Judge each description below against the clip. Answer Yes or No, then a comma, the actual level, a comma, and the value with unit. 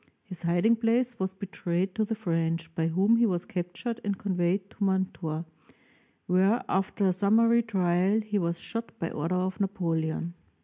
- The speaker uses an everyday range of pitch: Yes, average, 3.6 semitones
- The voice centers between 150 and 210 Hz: Yes, high, 190 Hz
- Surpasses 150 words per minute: Yes, average, 165 wpm